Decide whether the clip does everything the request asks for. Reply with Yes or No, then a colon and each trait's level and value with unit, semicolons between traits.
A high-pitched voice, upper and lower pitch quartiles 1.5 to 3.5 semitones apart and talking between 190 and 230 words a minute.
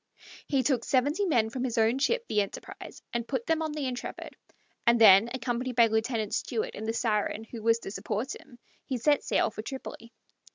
Yes: high, 235 Hz; average, 3.2 semitones; average, 200 wpm